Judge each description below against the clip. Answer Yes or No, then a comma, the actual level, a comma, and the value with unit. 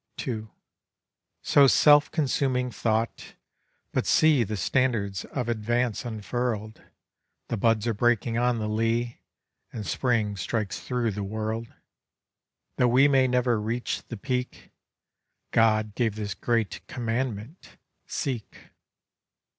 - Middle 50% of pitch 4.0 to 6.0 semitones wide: No, narrow, 2.6 semitones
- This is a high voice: No, low, 115 Hz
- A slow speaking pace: Yes, slow, 115 wpm